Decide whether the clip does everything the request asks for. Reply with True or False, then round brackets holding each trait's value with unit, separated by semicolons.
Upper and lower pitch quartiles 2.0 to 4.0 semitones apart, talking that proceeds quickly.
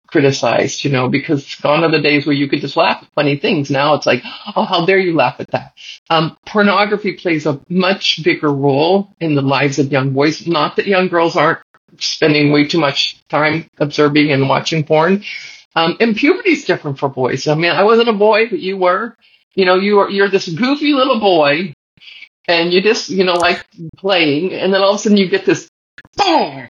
False (5.0 semitones; 215 wpm)